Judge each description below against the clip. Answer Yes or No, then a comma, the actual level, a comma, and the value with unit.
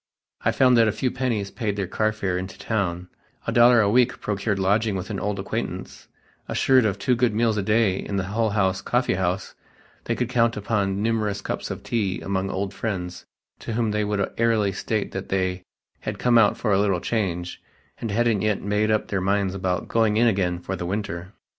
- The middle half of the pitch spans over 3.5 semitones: No, average, 2.9 semitones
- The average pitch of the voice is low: Yes, low, 105 Hz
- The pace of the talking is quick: Yes, fast, 210 wpm